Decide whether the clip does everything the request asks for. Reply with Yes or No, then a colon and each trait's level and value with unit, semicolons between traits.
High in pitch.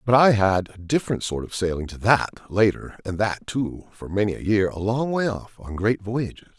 No: low, 105 Hz